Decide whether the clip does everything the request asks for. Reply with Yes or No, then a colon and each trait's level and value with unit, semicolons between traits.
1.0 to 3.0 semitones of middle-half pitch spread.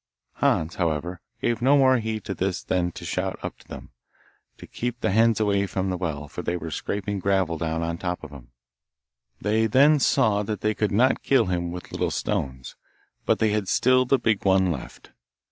No: average, 4.2 semitones